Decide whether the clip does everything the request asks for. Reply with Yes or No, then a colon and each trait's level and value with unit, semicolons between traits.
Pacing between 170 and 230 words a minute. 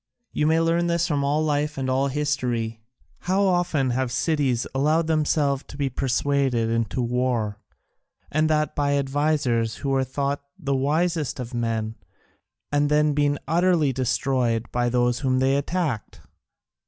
No: average, 150 wpm